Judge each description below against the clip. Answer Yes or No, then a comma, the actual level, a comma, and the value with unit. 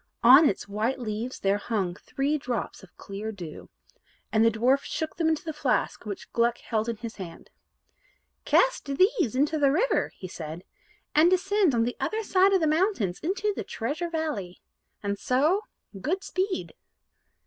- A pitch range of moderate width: No, wide, 7.7 semitones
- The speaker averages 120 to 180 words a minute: Yes, average, 170 wpm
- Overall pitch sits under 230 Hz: No, very high, 265 Hz